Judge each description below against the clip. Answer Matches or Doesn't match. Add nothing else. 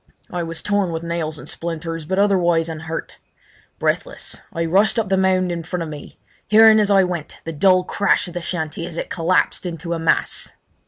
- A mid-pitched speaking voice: Matches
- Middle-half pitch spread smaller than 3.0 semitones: Matches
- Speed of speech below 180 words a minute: Doesn't match